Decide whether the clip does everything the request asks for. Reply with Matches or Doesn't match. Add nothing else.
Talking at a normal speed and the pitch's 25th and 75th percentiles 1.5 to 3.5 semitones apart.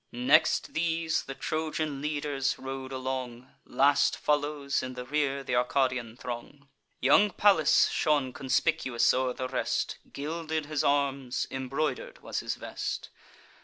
Doesn't match